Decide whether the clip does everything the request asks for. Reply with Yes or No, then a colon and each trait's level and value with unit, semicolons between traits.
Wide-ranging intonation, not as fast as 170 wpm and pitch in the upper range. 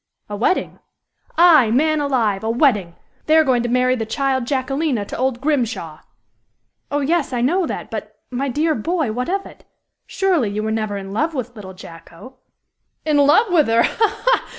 No: wide, 5.7 semitones; average, 185 wpm; very high, 260 Hz